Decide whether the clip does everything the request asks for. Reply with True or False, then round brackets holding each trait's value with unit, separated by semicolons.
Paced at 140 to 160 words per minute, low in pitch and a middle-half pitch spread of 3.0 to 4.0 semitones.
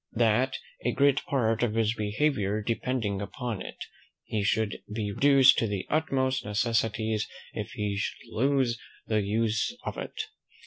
True (145 wpm; 115 Hz; 3.7 semitones)